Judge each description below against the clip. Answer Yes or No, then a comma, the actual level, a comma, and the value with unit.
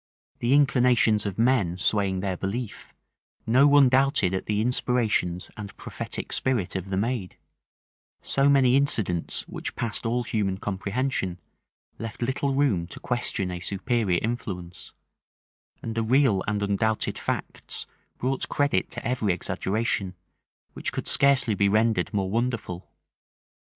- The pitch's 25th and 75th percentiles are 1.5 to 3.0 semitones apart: No, average, 4.7 semitones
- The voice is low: Yes, low, 110 Hz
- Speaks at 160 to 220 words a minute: No, slow, 135 wpm